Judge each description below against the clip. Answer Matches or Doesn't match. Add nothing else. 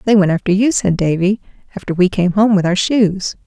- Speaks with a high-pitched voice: Matches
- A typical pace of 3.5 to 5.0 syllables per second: Doesn't match